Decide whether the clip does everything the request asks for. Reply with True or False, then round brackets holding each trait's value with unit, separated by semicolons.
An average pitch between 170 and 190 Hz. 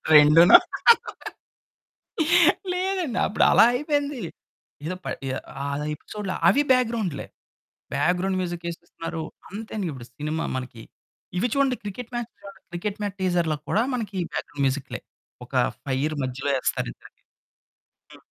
True (185 Hz)